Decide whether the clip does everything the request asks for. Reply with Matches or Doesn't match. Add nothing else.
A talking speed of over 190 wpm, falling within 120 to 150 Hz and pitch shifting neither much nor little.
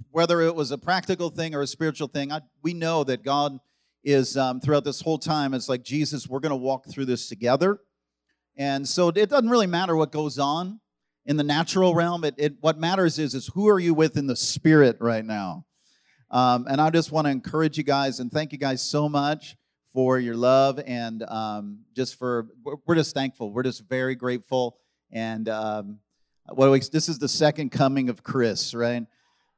Matches